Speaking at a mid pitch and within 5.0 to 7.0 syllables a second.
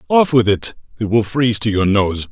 No: low, 110 Hz; 5.3 syllables/s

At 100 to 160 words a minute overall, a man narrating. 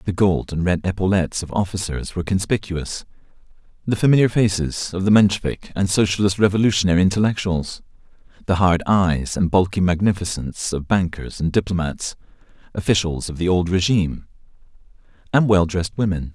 Yes: average, 140 wpm; male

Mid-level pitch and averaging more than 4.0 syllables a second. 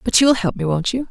No: high, 215 Hz; 5.9 syllables/s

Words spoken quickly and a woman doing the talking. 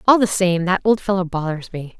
Yes: fast, 240 wpm; female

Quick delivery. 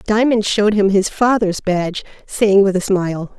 No: average, 175 wpm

